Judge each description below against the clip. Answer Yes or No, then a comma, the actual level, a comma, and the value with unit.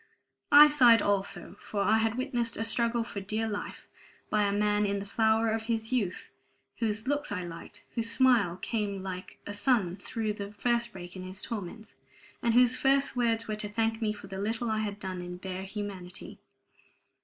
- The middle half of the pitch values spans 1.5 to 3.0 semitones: Yes, narrow, 2.5 semitones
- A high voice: Yes, high, 215 Hz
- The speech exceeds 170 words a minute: Yes, average, 190 wpm